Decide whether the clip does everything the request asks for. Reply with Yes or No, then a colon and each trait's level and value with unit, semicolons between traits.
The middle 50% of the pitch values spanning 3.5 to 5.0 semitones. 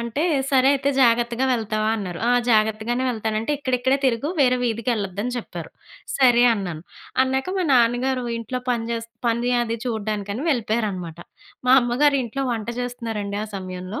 No: average, 2.8 semitones